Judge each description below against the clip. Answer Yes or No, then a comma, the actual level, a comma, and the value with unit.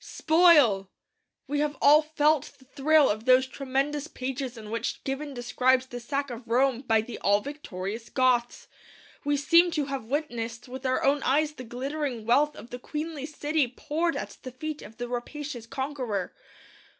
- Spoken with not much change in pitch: No, average, 3.5 semitones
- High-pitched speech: Yes, very high, 265 Hz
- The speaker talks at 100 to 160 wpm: No, average, 170 wpm